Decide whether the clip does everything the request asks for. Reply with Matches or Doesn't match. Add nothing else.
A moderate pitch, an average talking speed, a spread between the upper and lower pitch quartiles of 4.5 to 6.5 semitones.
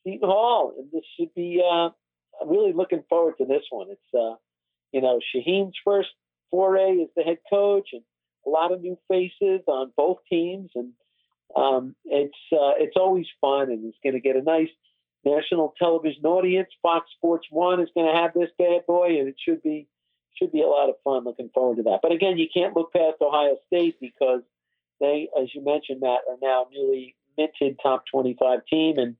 Matches